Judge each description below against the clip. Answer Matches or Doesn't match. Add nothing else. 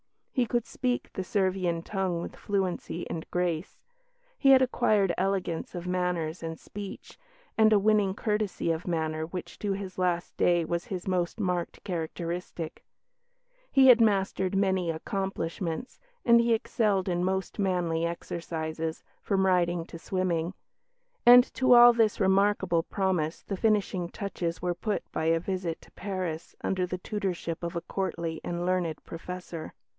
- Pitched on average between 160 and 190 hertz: Matches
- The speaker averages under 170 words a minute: Matches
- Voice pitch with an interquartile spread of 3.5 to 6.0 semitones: Doesn't match